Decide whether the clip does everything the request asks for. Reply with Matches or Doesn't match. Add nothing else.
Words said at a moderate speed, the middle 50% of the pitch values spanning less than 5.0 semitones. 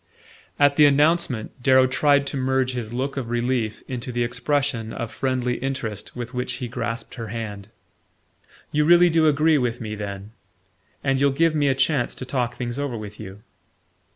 Matches